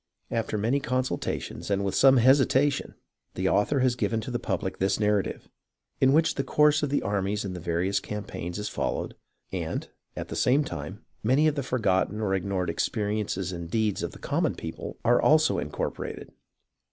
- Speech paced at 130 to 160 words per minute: No, average, 175 wpm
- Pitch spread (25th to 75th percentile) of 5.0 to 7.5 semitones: Yes, wide, 5.4 semitones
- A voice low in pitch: Yes, low, 110 Hz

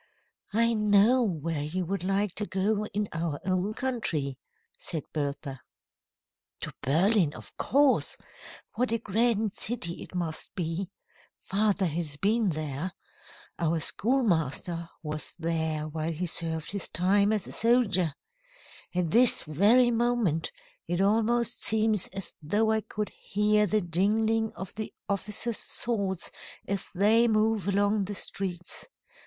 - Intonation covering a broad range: No, average, 4.6 semitones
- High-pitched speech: Yes, high, 195 Hz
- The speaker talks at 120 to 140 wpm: Yes, slow, 135 wpm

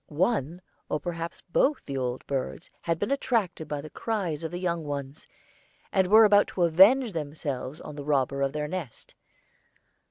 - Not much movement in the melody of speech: No, average, 4.6 semitones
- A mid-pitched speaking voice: Yes, medium, 165 Hz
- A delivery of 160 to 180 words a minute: Yes, average, 170 wpm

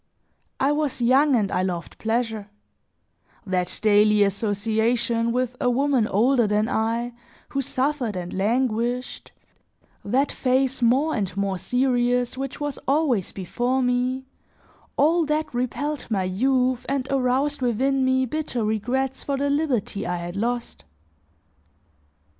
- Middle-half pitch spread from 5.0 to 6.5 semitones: No, average, 3.8 semitones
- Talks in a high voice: Yes, high, 245 Hz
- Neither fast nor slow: No, slow, 130 wpm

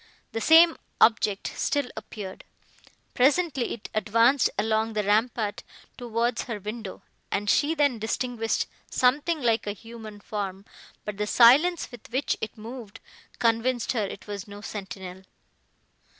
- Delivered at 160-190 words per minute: No, slow, 135 wpm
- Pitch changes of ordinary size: Yes, average, 3.2 semitones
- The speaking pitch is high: Yes, high, 225 Hz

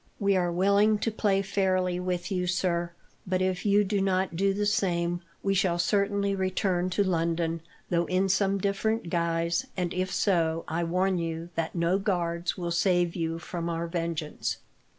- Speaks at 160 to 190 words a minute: Yes, average, 170 wpm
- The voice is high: No, medium, 180 Hz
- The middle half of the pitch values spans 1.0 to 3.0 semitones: Yes, narrow, 2.5 semitones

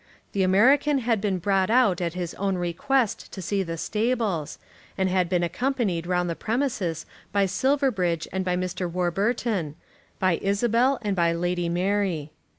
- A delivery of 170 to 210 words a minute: No, average, 155 wpm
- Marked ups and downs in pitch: No, average, 4.2 semitones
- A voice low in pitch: No, high, 190 Hz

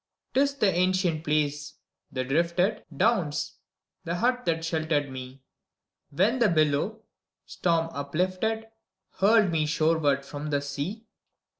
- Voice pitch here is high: No, medium, 165 Hz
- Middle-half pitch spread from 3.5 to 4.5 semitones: No, average, 5.3 semitones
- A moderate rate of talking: No, slow, 125 wpm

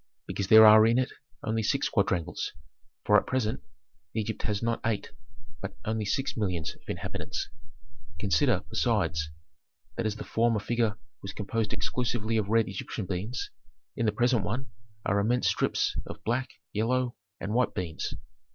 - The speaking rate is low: No, average, 155 wpm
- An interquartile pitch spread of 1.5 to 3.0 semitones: Yes, narrow, 2.5 semitones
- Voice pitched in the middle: No, low, 110 Hz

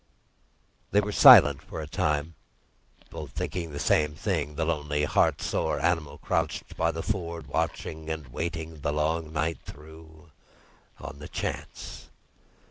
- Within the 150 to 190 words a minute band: No, slow, 135 wpm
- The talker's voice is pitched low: Yes, very low, 80 Hz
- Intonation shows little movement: Yes, narrow, 1.9 semitones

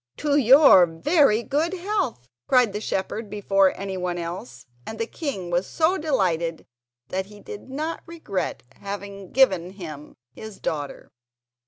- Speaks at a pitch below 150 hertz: No, high, 205 Hz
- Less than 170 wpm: Yes, average, 140 wpm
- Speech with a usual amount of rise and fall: No, wide, 7.5 semitones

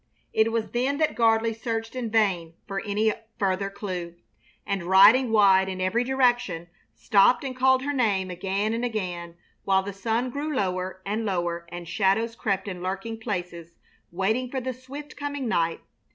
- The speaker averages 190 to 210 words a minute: No, average, 165 wpm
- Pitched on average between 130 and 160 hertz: No, high, 210 Hz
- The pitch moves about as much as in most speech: Yes, average, 4.4 semitones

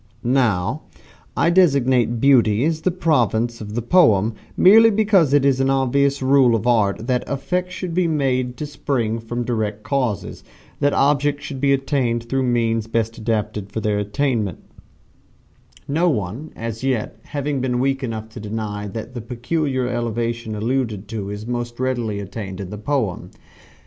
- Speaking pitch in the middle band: No, low, 120 Hz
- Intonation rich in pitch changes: No, average, 4.0 semitones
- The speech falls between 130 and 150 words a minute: No, average, 160 wpm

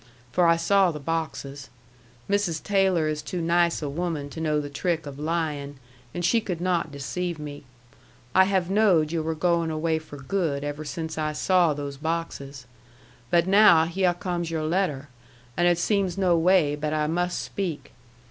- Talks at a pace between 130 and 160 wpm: No, average, 175 wpm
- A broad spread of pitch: No, average, 2.9 semitones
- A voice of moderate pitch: Yes, medium, 165 Hz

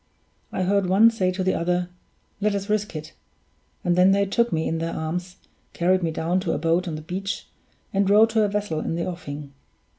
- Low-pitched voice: No, medium, 185 Hz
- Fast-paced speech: Yes, fast, 215 wpm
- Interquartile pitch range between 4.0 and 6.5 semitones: No, average, 3.1 semitones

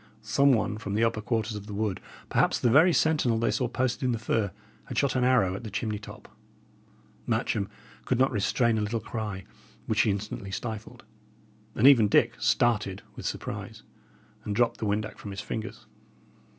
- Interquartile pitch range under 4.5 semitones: Yes, narrow, 2.6 semitones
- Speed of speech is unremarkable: Yes, average, 185 wpm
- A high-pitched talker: No, low, 110 Hz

